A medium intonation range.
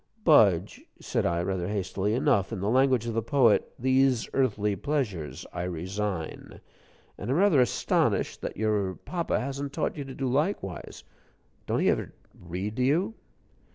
No: wide, 5.9 semitones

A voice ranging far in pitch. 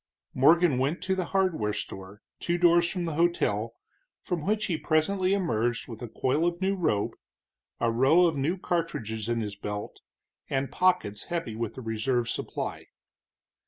Yes: wide, 7.4 semitones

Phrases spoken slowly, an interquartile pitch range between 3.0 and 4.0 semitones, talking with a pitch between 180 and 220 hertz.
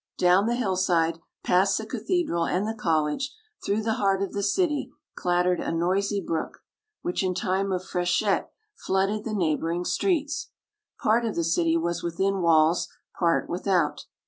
No: average, 155 wpm; average, 3.5 semitones; medium, 185 Hz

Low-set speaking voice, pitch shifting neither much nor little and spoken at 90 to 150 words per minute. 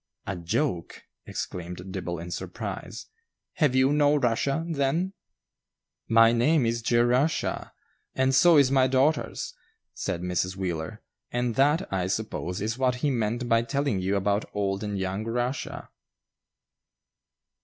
No: low, 120 Hz; wide, 5.8 semitones; slow, 135 wpm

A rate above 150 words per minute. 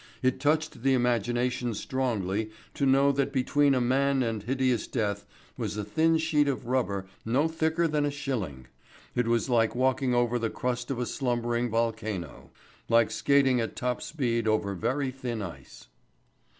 Yes: average, 165 wpm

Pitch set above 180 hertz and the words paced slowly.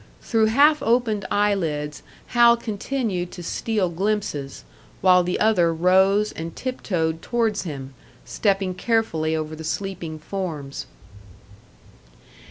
Yes: high, 190 Hz; slow, 120 wpm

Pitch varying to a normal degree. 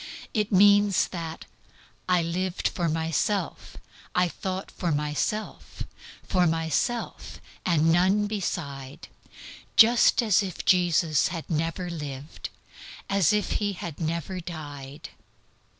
Yes: average, 3.4 semitones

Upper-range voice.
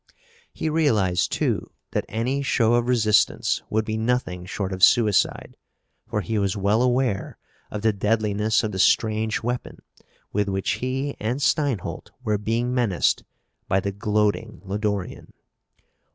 No: low, 110 Hz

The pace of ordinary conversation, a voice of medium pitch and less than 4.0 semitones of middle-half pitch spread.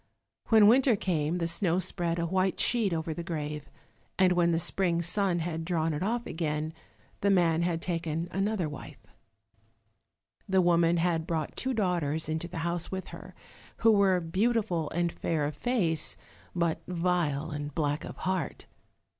Yes: average, 165 wpm; medium, 170 Hz; narrow, 2.6 semitones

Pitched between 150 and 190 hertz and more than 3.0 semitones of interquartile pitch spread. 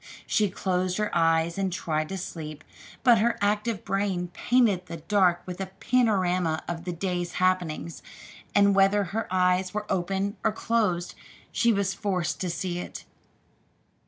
No: medium, 185 Hz; average, 2.7 semitones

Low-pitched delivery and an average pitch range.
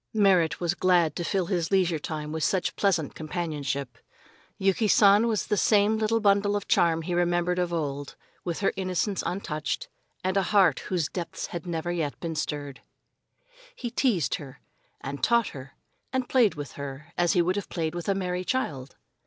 No: medium, 175 Hz; average, 4.1 semitones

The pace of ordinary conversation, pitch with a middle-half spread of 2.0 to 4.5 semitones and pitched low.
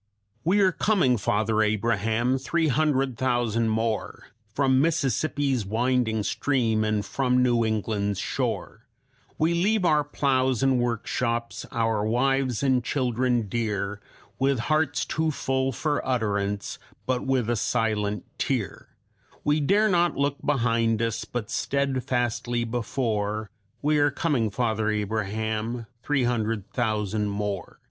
No: slow, 125 wpm; average, 3.7 semitones; low, 120 Hz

